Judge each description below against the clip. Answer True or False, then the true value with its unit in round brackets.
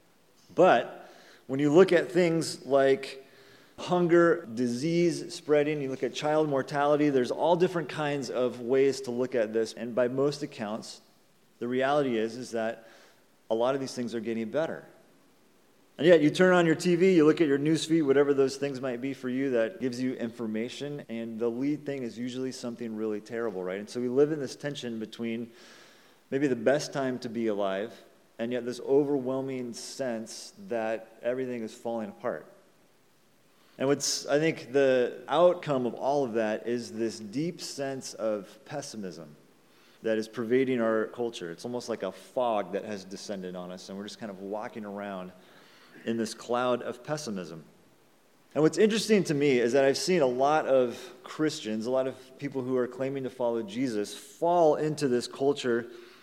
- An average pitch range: True (4.0 semitones)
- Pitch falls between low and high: False (130 Hz)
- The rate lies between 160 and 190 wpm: True (180 wpm)